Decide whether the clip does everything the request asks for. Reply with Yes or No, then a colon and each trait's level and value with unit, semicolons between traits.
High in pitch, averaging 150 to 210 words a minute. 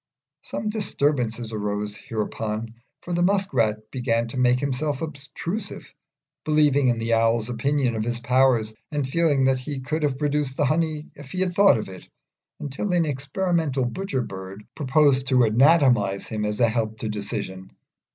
No: low, 130 Hz; average, 165 wpm